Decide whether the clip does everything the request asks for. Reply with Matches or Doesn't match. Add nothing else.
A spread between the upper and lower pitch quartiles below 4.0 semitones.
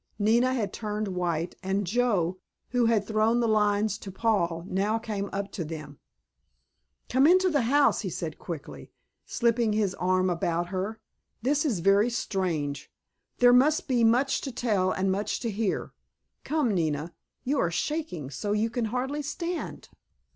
Doesn't match